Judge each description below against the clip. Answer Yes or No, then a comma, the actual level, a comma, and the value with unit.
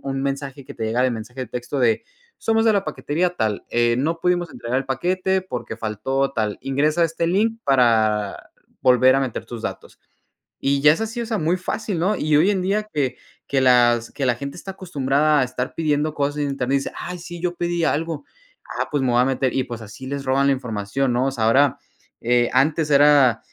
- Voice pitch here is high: No, medium, 140 Hz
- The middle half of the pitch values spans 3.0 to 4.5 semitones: No, average, 4.9 semitones